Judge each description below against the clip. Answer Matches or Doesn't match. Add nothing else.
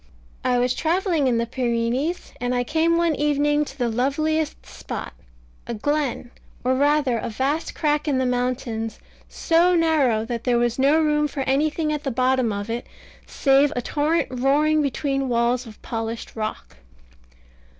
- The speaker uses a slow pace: Doesn't match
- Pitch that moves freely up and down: Doesn't match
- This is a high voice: Matches